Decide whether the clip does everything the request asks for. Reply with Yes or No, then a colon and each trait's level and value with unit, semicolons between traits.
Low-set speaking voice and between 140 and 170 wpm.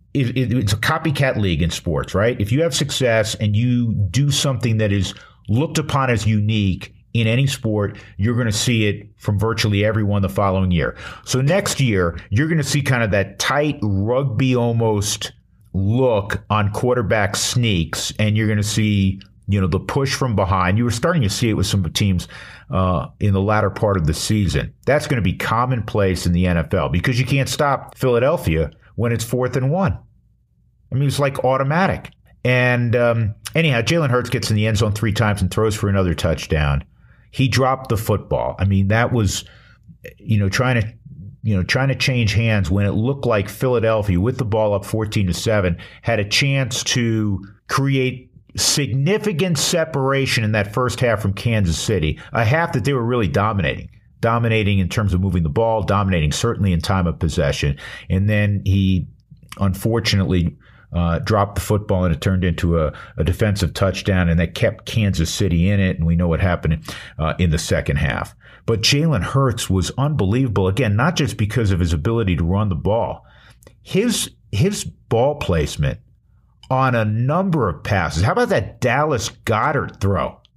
No: low, 110 Hz; average, 185 wpm